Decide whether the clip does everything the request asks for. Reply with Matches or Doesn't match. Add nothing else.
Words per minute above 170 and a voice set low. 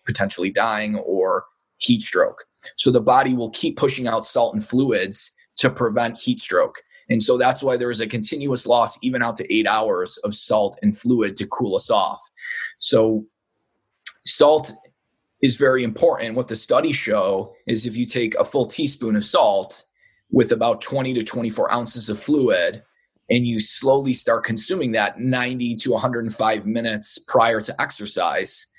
Doesn't match